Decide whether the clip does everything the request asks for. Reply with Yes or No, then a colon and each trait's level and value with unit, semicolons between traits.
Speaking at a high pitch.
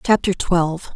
No: medium, 180 Hz